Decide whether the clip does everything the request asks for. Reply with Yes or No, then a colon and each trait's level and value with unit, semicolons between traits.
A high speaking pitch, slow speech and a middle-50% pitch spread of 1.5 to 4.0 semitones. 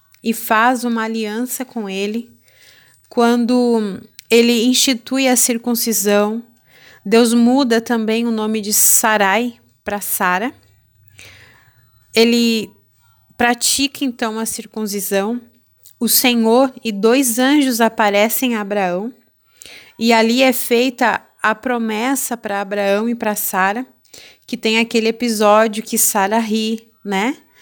Yes: high, 225 Hz; slow, 115 wpm; average, 2.7 semitones